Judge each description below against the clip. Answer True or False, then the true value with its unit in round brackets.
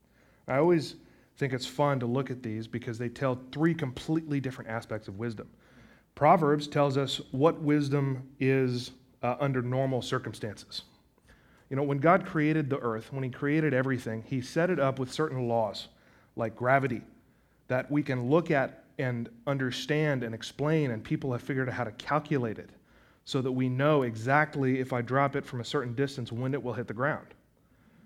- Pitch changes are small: False (3.0 semitones)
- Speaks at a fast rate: False (180 wpm)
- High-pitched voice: False (130 Hz)